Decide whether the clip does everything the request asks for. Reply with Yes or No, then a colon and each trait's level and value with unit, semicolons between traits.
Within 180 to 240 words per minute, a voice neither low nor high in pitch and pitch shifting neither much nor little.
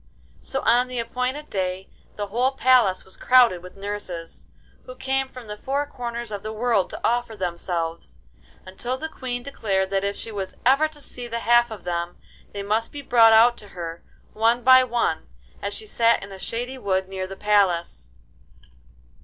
No: average, 185 wpm; high, 225 Hz; average, 4.5 semitones